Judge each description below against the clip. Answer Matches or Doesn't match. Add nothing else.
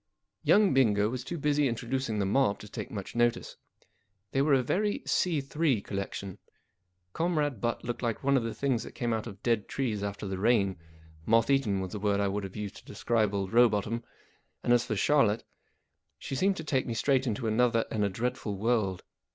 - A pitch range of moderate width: Matches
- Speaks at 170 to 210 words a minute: Matches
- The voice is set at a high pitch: Doesn't match